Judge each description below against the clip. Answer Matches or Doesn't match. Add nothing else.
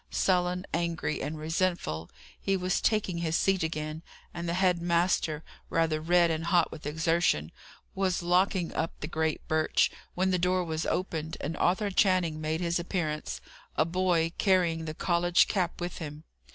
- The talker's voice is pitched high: Doesn't match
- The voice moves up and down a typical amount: Doesn't match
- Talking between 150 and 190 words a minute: Matches